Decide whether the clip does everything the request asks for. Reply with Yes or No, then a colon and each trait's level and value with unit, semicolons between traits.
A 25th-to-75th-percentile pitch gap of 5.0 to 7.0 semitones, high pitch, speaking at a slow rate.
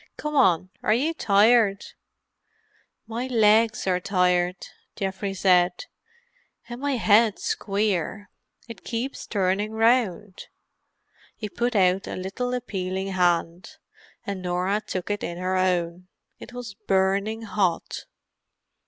No: average, 3.5 semitones; high, 200 Hz; slow, 115 wpm